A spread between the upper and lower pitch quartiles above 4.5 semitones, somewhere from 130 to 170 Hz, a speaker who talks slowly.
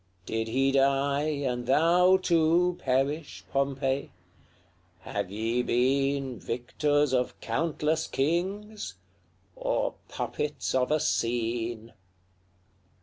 No: average, 4.1 semitones; medium, 140 Hz; slow, 90 wpm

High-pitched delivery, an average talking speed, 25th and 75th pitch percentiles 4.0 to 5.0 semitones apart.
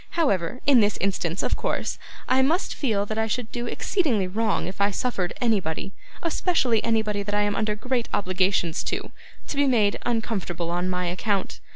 Yes: high, 210 Hz; average, 180 wpm; average, 4.3 semitones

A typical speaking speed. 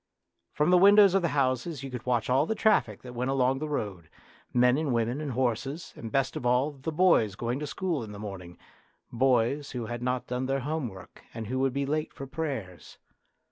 No: fast, 215 wpm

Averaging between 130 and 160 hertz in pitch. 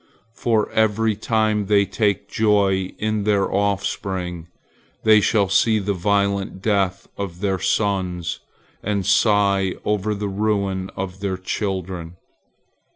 No: low, 100 Hz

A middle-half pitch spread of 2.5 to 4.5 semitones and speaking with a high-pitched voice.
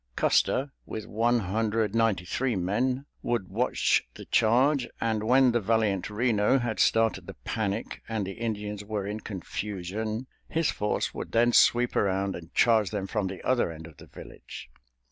No: average, 3.1 semitones; low, 110 Hz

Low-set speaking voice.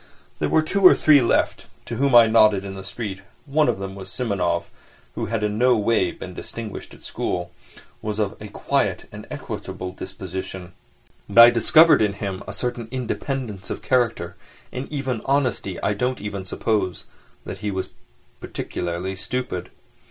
Yes: low, 105 Hz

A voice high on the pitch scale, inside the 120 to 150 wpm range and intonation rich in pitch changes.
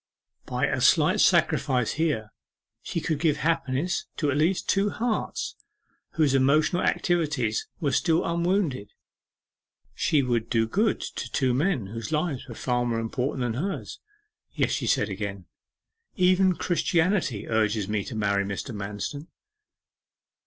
No: low, 135 Hz; average, 140 wpm; wide, 7.0 semitones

